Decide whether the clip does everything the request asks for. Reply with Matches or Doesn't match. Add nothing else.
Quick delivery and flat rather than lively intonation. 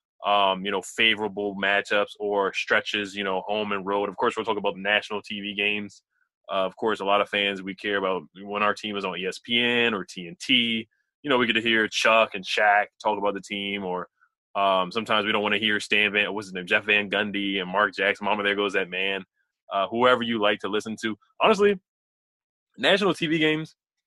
Matches